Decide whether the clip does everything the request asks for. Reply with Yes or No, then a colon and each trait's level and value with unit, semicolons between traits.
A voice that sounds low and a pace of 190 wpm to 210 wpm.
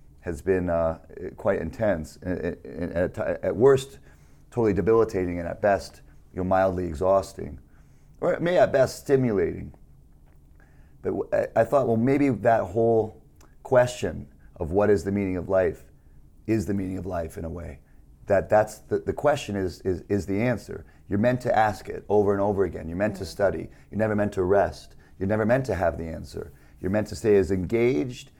No: very low, 95 Hz; average, 180 wpm